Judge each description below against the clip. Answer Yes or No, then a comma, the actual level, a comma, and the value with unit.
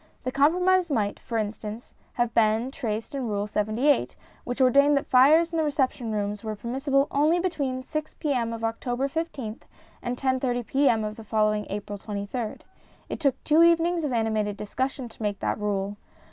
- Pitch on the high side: Yes, high, 245 Hz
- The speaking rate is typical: Yes, average, 175 wpm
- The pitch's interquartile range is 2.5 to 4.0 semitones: No, average, 4.8 semitones